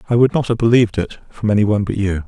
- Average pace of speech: No, fast, 290 wpm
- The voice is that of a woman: No, male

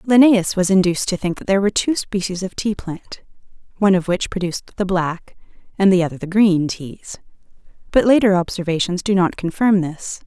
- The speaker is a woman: Yes, female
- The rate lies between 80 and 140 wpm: No, average, 185 wpm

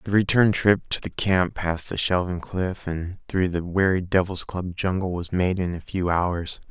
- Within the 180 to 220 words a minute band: Yes, fast, 205 wpm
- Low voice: Yes, very low, 90 Hz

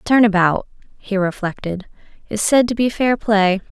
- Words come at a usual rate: Yes, average, 160 wpm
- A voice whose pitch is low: No, high, 210 Hz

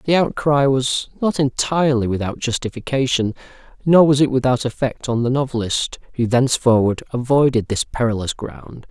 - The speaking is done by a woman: No, male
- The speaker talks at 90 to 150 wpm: Yes, average, 140 wpm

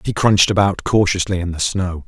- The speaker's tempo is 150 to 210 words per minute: Yes, fast, 205 wpm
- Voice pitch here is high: No, very low, 95 Hz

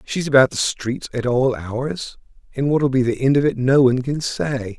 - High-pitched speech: No, low, 130 Hz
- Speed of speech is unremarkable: No, fast, 225 wpm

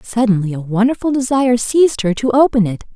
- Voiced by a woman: Yes, female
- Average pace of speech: Yes, average, 185 wpm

